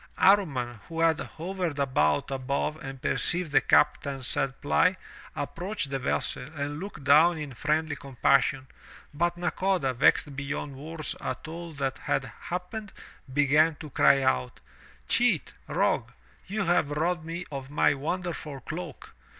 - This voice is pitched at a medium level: Yes, medium, 150 Hz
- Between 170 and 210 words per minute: No, average, 140 wpm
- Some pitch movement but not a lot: Yes, average, 4.0 semitones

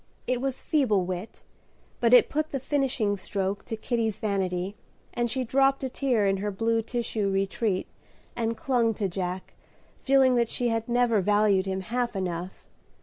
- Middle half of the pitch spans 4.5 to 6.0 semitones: No, average, 4.1 semitones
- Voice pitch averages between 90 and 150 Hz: No, high, 225 Hz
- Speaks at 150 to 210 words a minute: Yes, average, 165 wpm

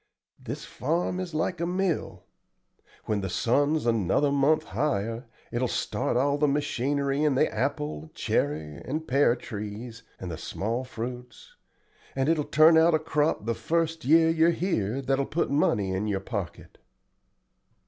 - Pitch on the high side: No, low, 135 Hz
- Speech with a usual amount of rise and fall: No, wide, 6.0 semitones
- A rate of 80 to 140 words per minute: No, average, 160 wpm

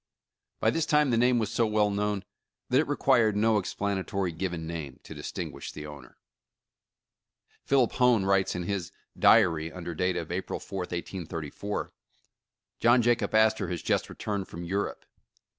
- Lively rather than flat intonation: No, average, 4.4 semitones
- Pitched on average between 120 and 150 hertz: No, low, 100 Hz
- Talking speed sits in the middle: Yes, average, 160 wpm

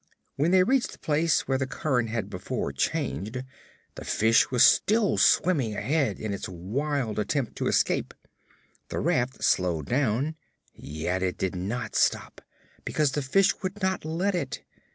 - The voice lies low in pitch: Yes, low, 130 Hz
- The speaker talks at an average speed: Yes, average, 155 wpm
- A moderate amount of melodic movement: No, wide, 7.0 semitones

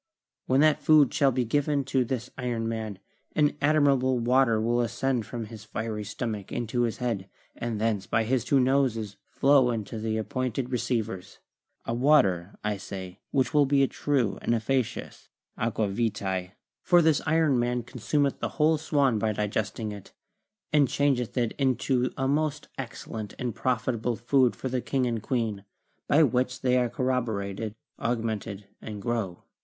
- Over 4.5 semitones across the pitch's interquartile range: No, average, 3.5 semitones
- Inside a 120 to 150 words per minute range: No, average, 160 wpm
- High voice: No, low, 120 Hz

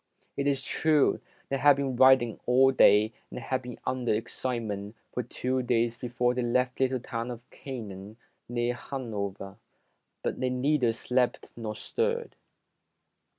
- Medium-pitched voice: No, low, 125 Hz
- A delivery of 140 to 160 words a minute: Yes, average, 150 wpm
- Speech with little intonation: Yes, narrow, 2.2 semitones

